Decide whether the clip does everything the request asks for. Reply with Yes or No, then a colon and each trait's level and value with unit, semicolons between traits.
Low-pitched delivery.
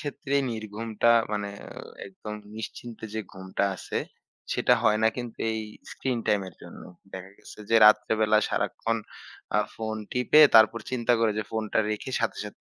Yes: low, 110 Hz